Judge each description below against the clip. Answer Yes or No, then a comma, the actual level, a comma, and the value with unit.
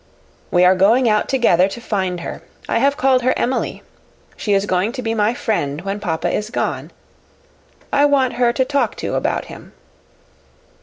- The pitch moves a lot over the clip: No, average, 5.0 semitones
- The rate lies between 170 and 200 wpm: Yes, average, 175 wpm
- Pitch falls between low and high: No, high, 225 Hz